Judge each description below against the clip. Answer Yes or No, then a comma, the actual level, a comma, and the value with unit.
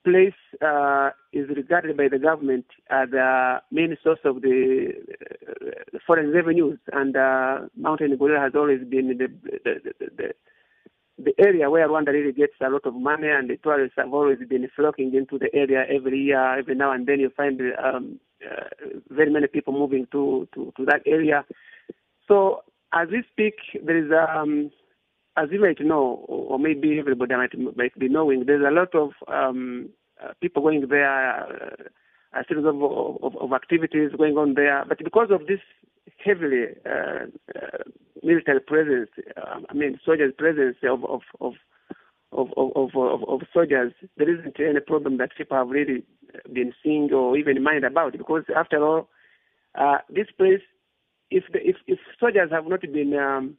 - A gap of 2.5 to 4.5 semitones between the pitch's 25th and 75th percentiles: No, average, 4.9 semitones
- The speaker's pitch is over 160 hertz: No, medium, 150 Hz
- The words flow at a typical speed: Yes, average, 170 wpm